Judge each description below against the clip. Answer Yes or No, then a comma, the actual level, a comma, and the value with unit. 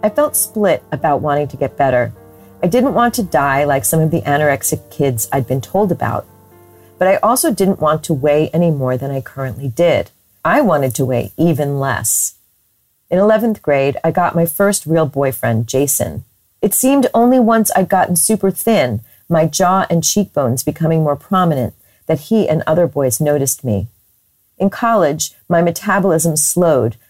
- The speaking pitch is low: No, medium, 150 Hz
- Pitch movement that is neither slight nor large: No, wide, 6.1 semitones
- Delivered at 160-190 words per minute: Yes, average, 175 wpm